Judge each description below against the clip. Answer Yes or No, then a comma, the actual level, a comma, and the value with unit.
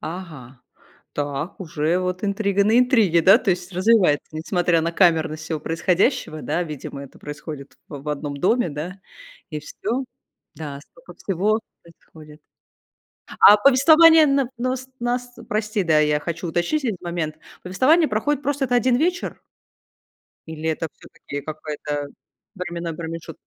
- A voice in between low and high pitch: Yes, medium, 175 Hz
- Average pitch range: No, wide, 6.8 semitones